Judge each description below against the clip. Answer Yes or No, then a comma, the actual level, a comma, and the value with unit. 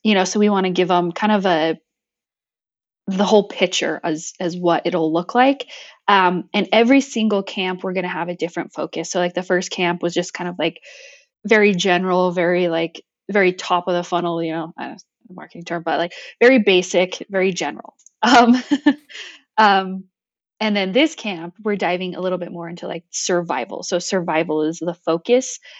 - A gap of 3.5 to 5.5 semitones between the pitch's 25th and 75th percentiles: No, average, 3.1 semitones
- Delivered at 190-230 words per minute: Yes, average, 200 wpm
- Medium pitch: Yes, medium, 180 Hz